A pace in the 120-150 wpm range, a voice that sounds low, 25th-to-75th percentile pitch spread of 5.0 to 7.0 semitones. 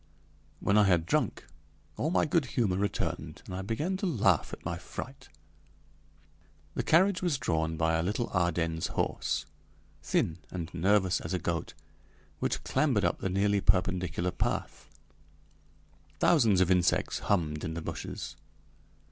Yes: average, 145 wpm; very low, 95 Hz; wide, 5.6 semitones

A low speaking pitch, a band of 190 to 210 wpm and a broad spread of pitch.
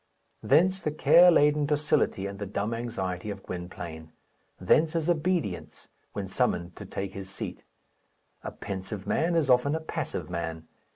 No: low, 105 Hz; average, 155 wpm; wide, 8.6 semitones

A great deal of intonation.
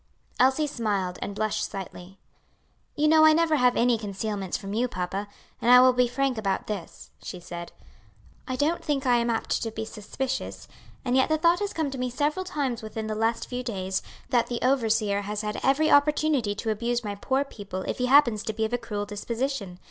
No: average, 4.4 semitones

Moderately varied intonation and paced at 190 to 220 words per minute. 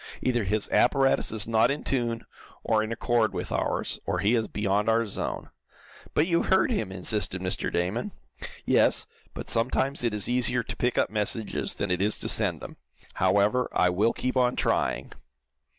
No: average, 3.5 semitones; average, 180 wpm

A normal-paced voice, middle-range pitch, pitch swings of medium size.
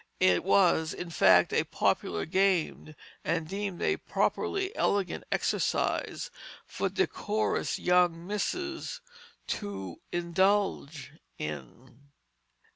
No: slow, 95 wpm; medium, 180 Hz; average, 4.5 semitones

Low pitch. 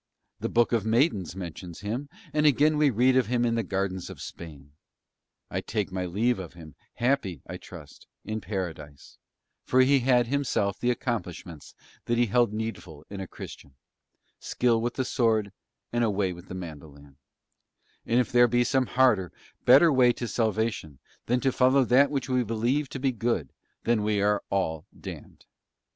Yes: low, 115 Hz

